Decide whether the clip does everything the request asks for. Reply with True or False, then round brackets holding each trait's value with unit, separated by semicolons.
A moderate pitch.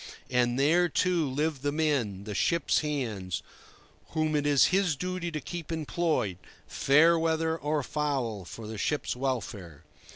True (145 Hz)